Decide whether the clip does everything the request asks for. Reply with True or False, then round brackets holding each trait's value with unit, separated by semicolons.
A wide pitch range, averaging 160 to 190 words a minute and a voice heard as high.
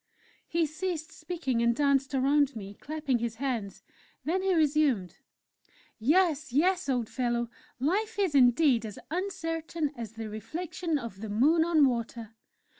False (5.7 semitones; 140 wpm; 280 Hz)